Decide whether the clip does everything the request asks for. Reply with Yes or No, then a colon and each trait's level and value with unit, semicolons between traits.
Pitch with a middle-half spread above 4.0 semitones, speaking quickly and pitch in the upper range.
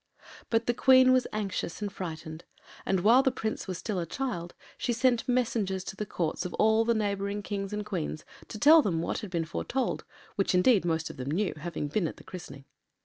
Yes: average, 4.9 semitones; fast, 210 wpm; high, 200 Hz